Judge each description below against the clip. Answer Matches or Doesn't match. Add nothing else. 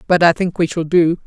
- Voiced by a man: Doesn't match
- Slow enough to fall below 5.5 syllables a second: Doesn't match